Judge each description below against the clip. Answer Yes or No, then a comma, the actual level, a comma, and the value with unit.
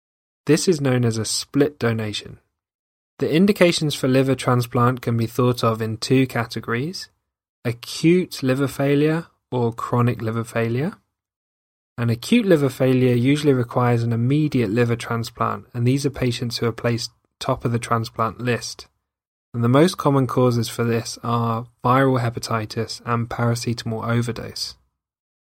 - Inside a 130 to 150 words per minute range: Yes, average, 145 wpm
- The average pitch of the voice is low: Yes, low, 120 Hz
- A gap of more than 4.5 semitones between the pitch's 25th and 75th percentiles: No, narrow, 2.5 semitones